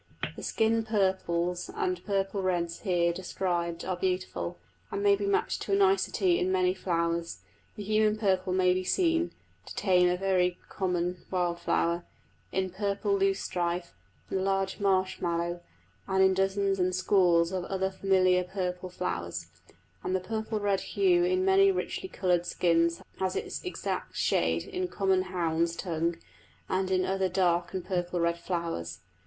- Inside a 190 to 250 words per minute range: No, average, 160 wpm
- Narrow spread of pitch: Yes, narrow, 2.0 semitones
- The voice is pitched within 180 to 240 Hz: Yes, medium, 185 Hz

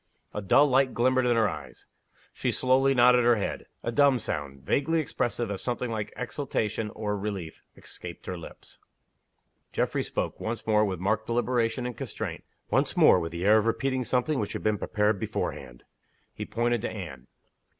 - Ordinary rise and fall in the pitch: Yes, average, 3.4 semitones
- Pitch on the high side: No, low, 115 Hz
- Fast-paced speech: No, average, 175 wpm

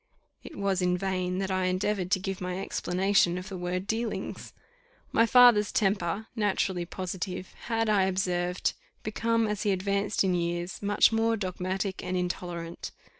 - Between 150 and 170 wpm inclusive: Yes, average, 155 wpm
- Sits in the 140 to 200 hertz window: Yes, high, 190 Hz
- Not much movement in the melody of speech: Yes, narrow, 2.3 semitones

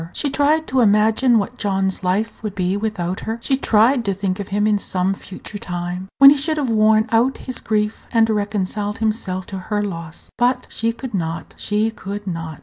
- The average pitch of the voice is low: No, high, 210 Hz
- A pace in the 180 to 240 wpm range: Yes, average, 200 wpm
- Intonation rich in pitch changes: No, average, 3.1 semitones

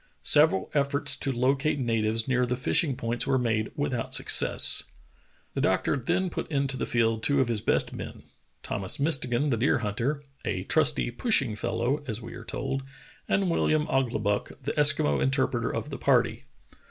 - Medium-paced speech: Yes, average, 165 wpm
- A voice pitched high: No, low, 130 Hz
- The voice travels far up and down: No, average, 3.8 semitones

